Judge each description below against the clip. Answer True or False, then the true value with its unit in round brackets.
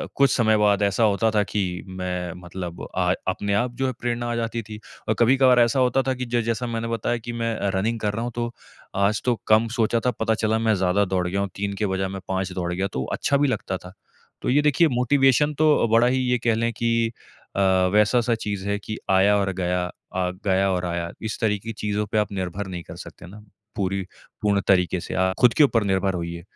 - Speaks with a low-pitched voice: True (105 Hz)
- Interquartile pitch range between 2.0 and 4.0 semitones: True (3.7 semitones)